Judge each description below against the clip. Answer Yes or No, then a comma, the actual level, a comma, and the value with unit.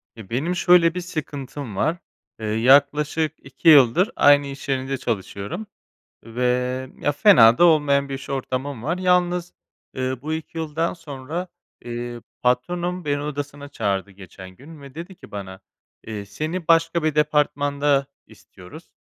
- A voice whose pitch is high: No, medium, 145 Hz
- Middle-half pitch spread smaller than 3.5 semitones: No, average, 4.7 semitones